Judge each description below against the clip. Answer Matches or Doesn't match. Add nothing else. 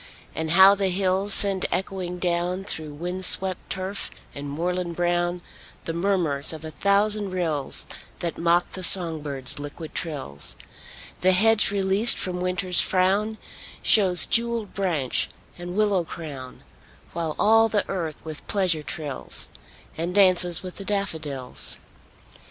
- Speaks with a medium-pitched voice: Matches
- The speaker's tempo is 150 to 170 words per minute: Doesn't match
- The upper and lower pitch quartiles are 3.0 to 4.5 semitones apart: Matches